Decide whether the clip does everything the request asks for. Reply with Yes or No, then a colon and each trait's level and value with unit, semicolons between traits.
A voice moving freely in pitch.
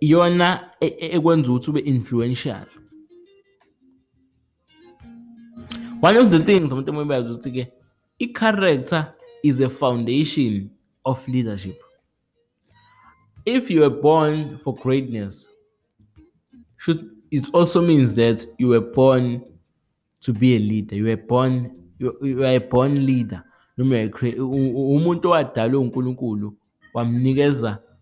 Yes: wide, 5.7 semitones